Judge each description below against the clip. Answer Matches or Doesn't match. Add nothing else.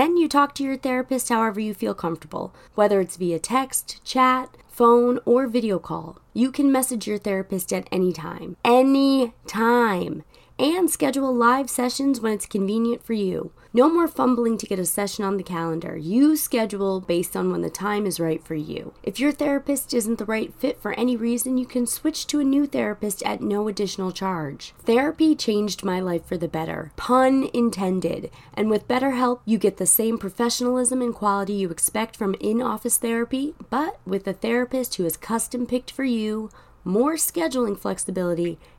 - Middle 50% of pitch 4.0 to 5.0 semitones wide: Matches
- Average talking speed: Matches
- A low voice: Doesn't match